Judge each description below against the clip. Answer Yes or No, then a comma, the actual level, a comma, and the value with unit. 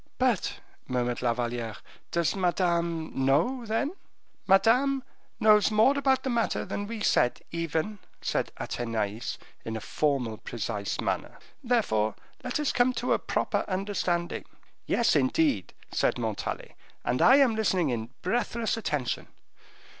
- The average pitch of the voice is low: No, medium, 185 Hz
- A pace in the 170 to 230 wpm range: No, slow, 135 wpm